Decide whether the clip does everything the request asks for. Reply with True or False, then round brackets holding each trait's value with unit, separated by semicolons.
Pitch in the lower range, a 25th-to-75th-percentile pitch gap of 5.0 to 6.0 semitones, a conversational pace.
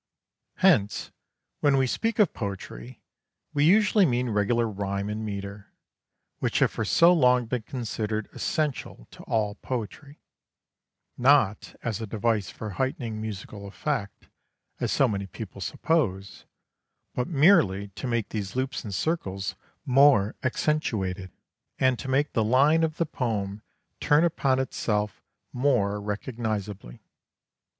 False (115 Hz; 5.3 semitones; 130 wpm)